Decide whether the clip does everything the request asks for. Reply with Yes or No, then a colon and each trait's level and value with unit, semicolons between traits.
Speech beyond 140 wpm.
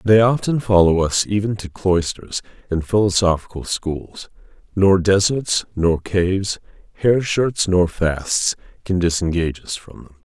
No: slow, 135 wpm